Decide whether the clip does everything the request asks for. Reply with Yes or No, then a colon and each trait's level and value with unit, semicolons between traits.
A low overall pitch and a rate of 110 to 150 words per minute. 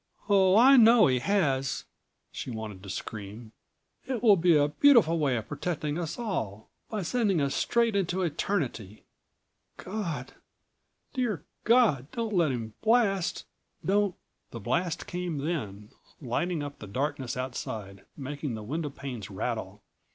No: medium, 155 Hz; average, 140 wpm